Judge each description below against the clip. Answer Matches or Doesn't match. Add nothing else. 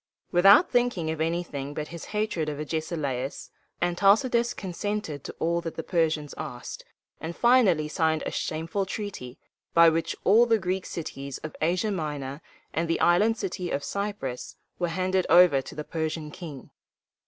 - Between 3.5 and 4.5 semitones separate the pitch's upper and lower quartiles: Matches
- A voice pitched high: Doesn't match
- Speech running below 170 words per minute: Matches